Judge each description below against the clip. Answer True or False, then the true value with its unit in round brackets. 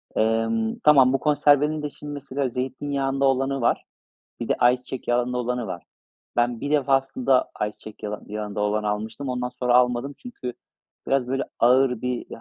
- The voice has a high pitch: False (125 Hz)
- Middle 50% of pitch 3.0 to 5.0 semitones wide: False (2.6 semitones)